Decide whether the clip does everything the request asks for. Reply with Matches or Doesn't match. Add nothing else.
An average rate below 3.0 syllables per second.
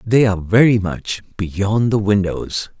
Doesn't match